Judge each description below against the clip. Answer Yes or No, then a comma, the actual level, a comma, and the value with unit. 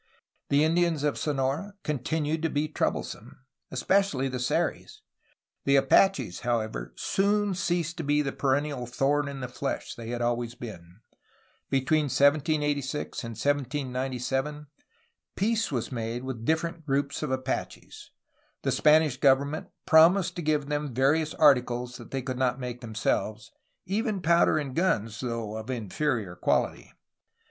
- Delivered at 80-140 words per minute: Yes, slow, 135 wpm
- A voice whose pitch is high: No, medium, 140 Hz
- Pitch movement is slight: No, average, 4.0 semitones